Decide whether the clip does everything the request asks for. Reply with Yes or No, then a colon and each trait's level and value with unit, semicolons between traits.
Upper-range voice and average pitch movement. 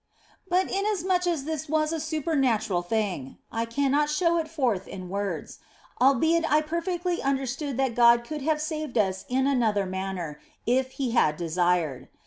No: very high, 270 Hz; wide, 7.3 semitones